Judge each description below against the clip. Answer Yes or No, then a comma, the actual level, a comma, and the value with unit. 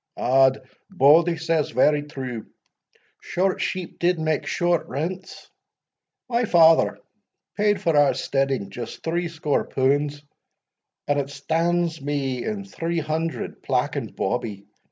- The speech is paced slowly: Yes, slow, 120 wpm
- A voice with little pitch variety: No, average, 3.9 semitones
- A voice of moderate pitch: Yes, medium, 155 Hz